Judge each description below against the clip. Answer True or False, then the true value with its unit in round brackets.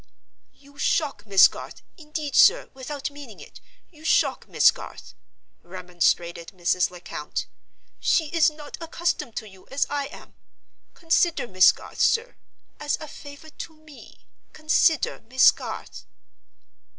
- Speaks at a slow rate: True (130 wpm)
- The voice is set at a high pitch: True (285 Hz)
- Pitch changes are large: True (7.6 semitones)